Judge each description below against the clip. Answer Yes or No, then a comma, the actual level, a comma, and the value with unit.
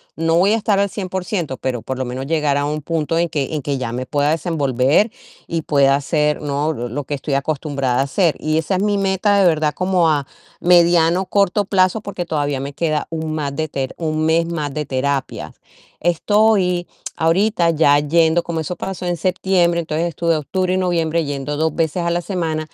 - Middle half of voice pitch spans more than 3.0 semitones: Yes, average, 3.6 semitones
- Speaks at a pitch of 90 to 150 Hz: No, medium, 160 Hz